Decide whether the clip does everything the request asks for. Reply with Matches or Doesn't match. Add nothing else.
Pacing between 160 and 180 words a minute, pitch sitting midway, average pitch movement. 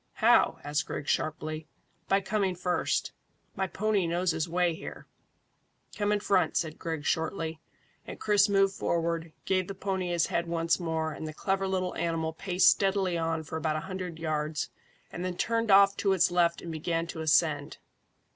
Matches